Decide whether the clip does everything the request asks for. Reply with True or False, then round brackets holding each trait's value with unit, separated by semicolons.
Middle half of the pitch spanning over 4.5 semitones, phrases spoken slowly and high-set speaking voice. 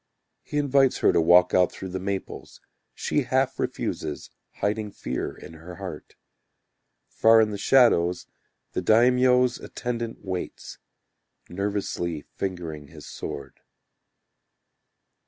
False (5.4 semitones; 115 wpm; 100 Hz)